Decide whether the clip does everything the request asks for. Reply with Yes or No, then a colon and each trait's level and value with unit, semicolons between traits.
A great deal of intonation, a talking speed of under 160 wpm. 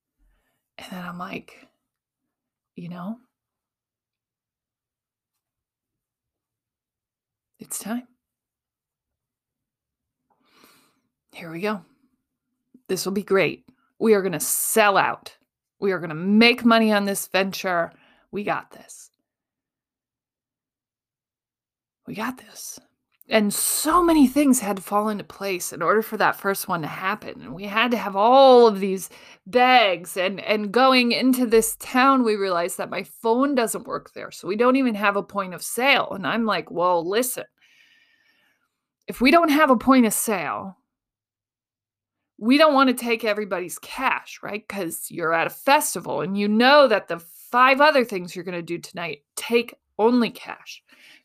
Yes: wide, 6.2 semitones; average, 150 wpm